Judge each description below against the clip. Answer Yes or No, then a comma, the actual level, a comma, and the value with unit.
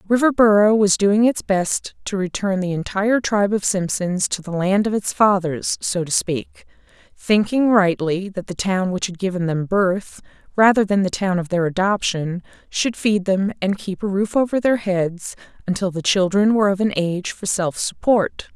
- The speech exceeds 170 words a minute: Yes, average, 190 wpm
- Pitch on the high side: Yes, high, 195 Hz